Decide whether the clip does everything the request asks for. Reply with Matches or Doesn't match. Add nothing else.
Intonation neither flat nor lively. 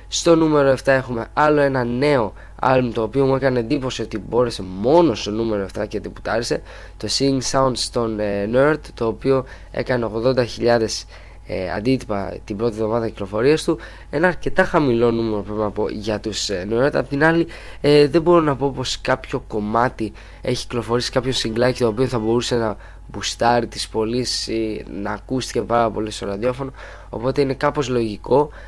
Matches